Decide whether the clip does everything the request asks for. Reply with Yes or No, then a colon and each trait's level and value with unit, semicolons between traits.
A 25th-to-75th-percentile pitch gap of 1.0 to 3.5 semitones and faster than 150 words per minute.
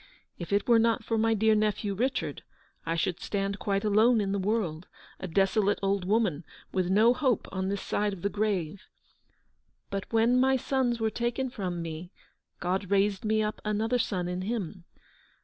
Yes: average, 3.1 semitones; average, 180 wpm